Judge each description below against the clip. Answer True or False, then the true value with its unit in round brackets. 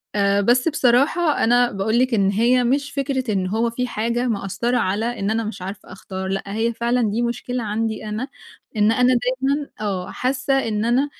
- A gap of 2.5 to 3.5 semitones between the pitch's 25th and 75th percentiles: True (3.2 semitones)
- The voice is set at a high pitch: True (235 Hz)